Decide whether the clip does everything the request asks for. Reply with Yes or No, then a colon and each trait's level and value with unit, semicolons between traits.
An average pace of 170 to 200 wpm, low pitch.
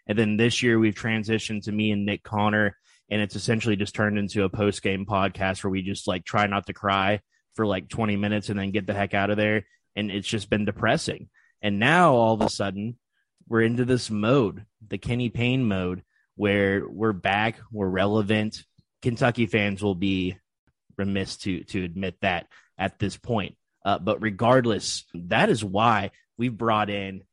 Yes: average, 190 wpm; low, 105 Hz